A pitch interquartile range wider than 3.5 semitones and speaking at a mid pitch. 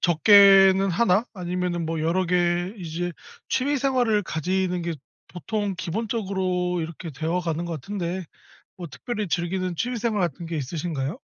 No: average, 2.8 semitones; medium, 180 Hz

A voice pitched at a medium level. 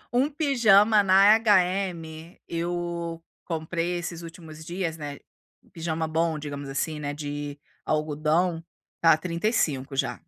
Yes: medium, 165 Hz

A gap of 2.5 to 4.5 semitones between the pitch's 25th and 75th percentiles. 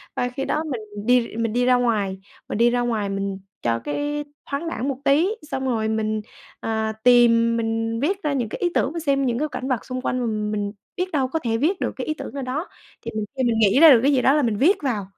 Yes: average, 4.0 semitones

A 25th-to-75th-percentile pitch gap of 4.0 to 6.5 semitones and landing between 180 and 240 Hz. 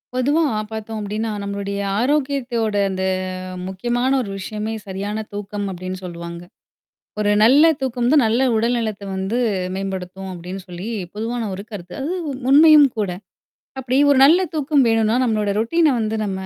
Yes: average, 4.6 semitones; high, 220 Hz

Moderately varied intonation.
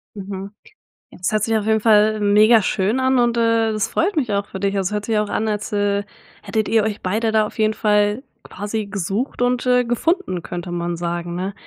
No: narrow, 2.2 semitones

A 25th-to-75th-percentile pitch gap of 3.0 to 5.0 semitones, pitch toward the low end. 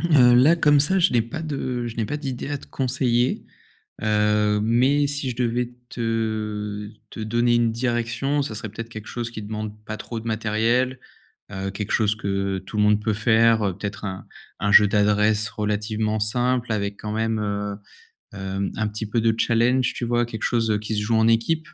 No: narrow, 2.5 semitones; low, 110 Hz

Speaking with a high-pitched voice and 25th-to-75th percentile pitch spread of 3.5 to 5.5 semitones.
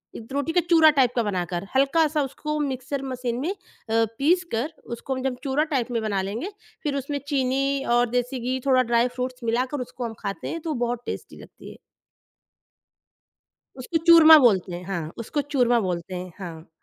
Yes: very high, 255 Hz; average, 3.8 semitones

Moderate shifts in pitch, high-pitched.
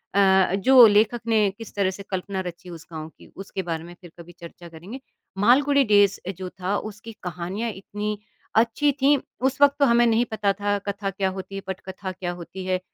Yes: average, 3.7 semitones; high, 195 Hz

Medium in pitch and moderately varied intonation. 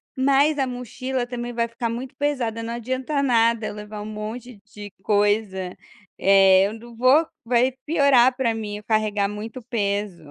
No: high, 230 Hz; average, 3.5 semitones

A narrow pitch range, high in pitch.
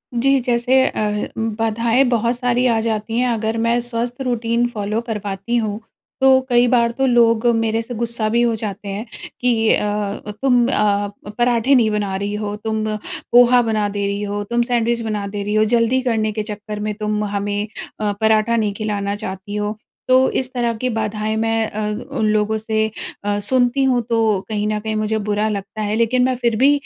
Yes: narrow, 2.2 semitones; high, 220 Hz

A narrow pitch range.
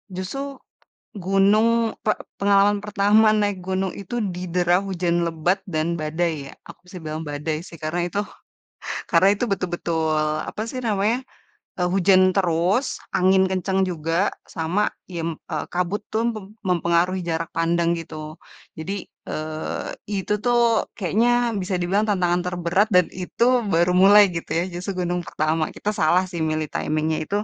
No: average, 3.2 semitones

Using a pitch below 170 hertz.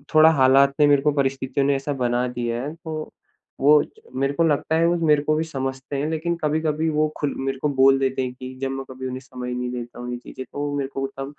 Yes: low, 135 Hz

